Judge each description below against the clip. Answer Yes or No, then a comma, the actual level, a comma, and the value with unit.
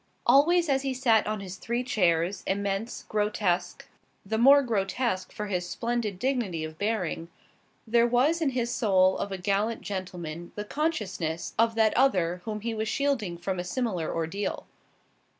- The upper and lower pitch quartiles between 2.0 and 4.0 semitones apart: No, average, 4.6 semitones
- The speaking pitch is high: Yes, high, 210 Hz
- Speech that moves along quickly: No, average, 160 wpm